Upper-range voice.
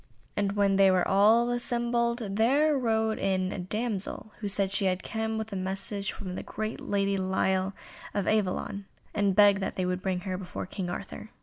Yes: high, 200 Hz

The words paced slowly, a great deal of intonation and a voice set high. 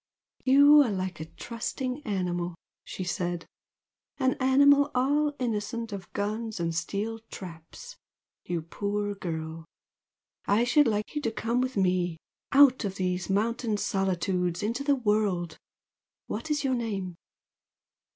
Yes: slow, 130 wpm; wide, 5.8 semitones; high, 210 Hz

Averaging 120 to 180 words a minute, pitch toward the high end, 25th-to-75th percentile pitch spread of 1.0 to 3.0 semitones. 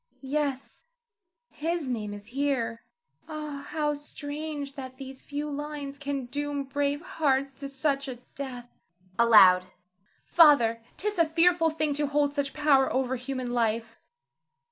Yes: average, 140 wpm; very high, 280 Hz; narrow, 2.4 semitones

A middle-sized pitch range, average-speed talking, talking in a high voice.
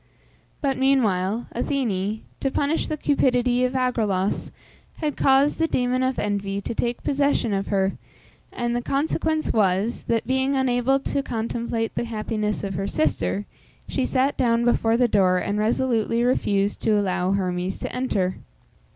Yes: average, 4.7 semitones; average, 150 wpm; high, 235 Hz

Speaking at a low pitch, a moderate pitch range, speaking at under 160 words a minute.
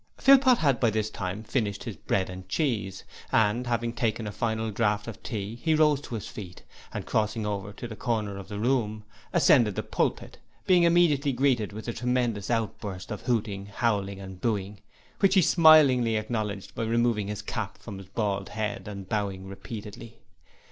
No: low, 110 Hz; average, 3.0 semitones; average, 180 wpm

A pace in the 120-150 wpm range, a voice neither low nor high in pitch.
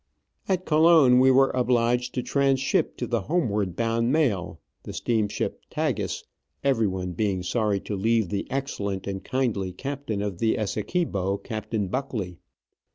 No: average, 140 wpm; low, 115 Hz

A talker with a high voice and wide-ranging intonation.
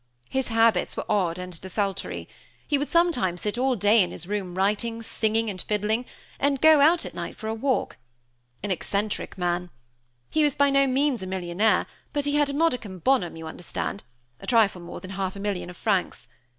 Yes: high, 210 Hz; wide, 6.1 semitones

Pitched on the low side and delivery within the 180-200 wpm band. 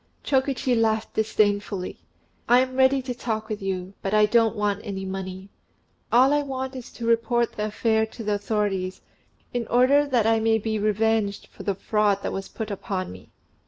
No: high, 220 Hz; average, 185 wpm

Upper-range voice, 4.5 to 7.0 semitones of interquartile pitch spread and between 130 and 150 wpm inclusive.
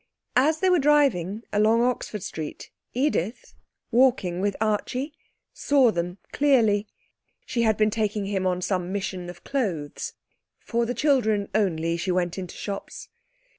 Yes: high, 210 Hz; average, 5.2 semitones; average, 140 wpm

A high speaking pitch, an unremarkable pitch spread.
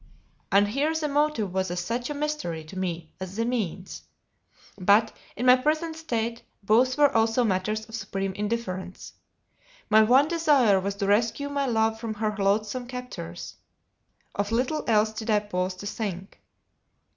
Yes: high, 220 Hz; average, 4.3 semitones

